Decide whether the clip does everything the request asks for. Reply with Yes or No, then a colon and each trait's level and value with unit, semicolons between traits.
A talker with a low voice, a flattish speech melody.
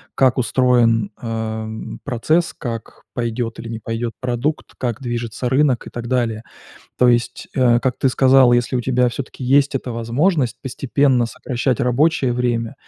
Yes: low, 125 Hz; narrow, 2.1 semitones